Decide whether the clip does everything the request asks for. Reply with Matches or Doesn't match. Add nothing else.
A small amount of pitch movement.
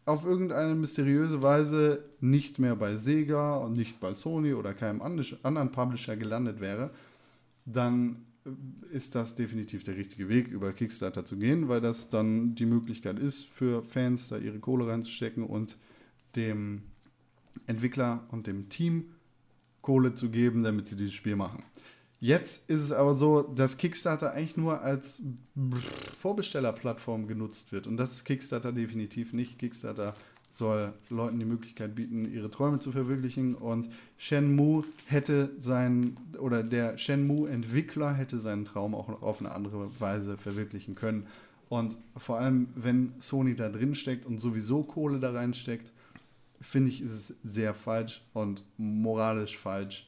Doesn't match